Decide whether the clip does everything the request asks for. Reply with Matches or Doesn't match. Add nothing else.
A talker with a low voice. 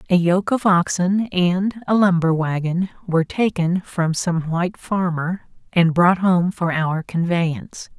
Doesn't match